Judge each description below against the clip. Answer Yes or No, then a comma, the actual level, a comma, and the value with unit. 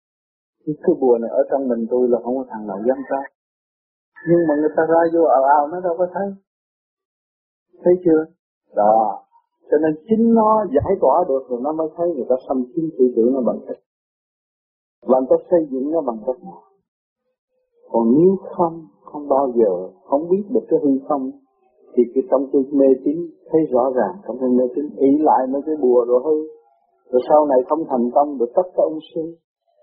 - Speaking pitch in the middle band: Yes, medium, 155 Hz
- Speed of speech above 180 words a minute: Yes, average, 205 wpm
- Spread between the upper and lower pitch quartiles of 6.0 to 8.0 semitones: No, average, 5.2 semitones